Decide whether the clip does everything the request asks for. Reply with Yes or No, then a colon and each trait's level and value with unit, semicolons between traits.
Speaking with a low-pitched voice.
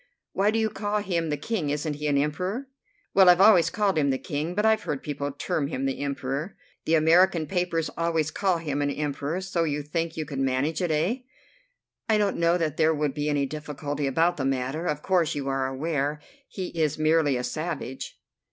No: medium, 155 Hz